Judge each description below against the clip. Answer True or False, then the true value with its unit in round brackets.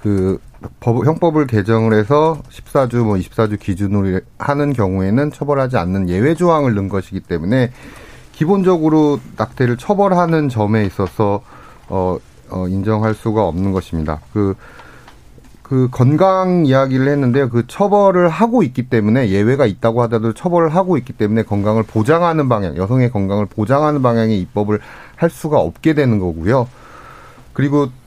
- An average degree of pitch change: False (6.1 semitones)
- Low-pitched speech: True (120 Hz)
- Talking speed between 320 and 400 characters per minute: True (325 characters per minute)